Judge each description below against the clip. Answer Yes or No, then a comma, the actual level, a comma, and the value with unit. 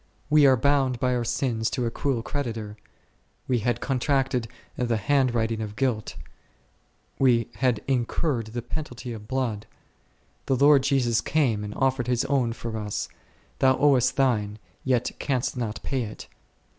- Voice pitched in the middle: No, low, 125 Hz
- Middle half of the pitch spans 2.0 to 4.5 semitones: Yes, average, 2.8 semitones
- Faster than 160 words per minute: No, average, 155 wpm